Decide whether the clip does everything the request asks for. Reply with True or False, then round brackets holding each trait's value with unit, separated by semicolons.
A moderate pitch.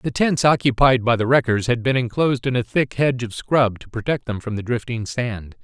False (120 Hz)